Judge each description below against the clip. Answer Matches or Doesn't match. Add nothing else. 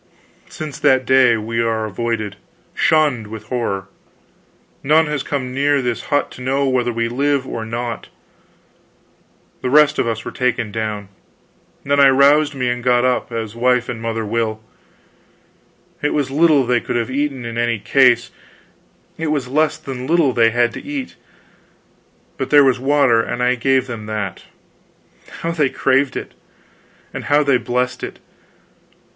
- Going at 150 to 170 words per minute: Matches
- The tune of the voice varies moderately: Matches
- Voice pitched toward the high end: Doesn't match